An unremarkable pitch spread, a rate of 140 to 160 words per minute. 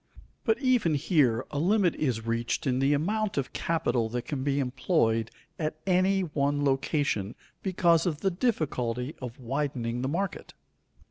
No: wide, 5.7 semitones; average, 150 wpm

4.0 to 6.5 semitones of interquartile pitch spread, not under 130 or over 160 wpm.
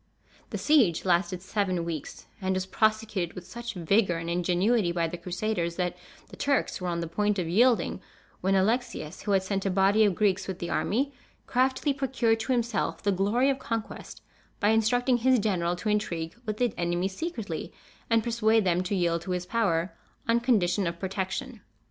No: average, 4.3 semitones; average, 185 wpm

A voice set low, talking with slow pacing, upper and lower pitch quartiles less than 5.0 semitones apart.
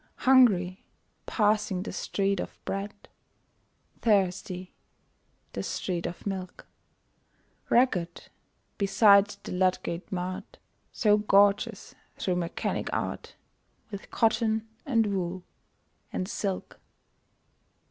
No: high, 195 Hz; slow, 90 wpm; narrow, 2.4 semitones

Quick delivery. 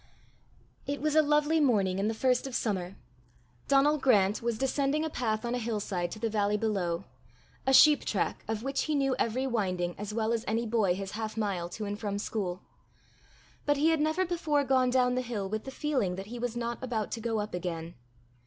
Yes: fast, 210 wpm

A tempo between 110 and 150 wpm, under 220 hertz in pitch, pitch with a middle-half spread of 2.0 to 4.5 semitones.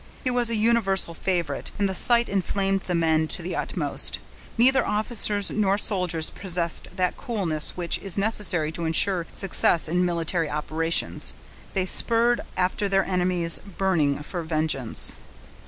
Yes: average, 145 wpm; medium, 185 Hz; average, 3.5 semitones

